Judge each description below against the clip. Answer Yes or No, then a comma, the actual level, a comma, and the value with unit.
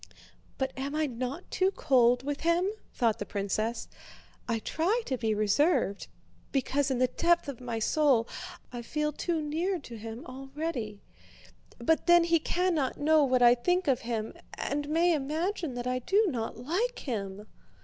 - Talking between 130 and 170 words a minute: Yes, average, 165 wpm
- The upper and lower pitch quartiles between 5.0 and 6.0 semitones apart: Yes, average, 5.3 semitones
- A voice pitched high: Yes, very high, 270 Hz